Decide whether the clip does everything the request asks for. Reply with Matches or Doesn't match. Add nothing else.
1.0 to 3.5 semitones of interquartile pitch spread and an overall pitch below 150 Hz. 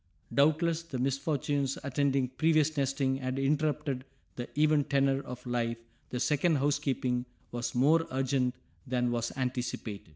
Matches